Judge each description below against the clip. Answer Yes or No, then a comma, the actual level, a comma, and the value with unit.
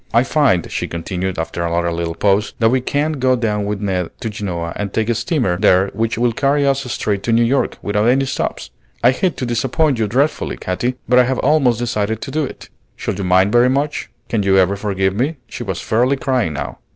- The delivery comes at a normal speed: No, fast, 225 wpm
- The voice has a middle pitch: No, low, 115 Hz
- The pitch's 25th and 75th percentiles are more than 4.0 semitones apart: Yes, average, 5.0 semitones